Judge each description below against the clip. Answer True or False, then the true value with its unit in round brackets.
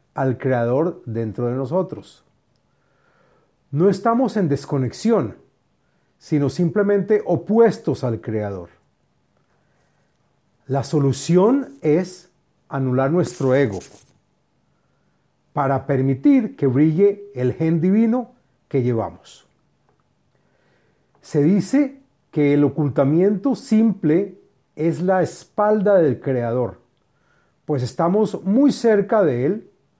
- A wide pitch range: True (7.2 semitones)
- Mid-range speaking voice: True (155 Hz)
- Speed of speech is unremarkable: False (90 wpm)